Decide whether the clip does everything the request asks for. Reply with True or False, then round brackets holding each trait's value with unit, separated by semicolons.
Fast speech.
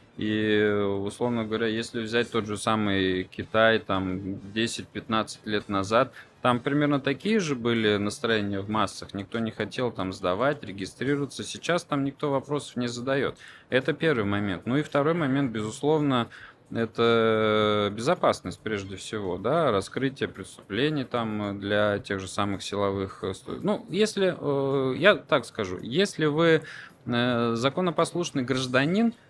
False (130 wpm)